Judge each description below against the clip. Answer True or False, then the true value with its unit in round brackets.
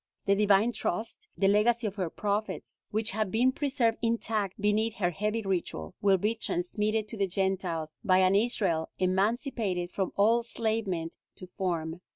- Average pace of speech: True (160 wpm)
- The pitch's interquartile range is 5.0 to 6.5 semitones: False (3.2 semitones)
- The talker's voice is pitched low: False (205 Hz)